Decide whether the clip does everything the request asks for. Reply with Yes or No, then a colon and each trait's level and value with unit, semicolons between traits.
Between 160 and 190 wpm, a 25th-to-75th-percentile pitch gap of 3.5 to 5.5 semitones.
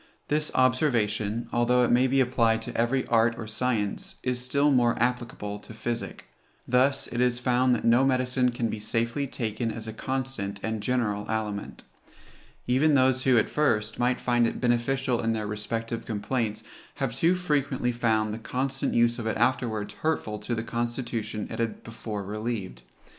No: average, 170 wpm; narrow, 2.5 semitones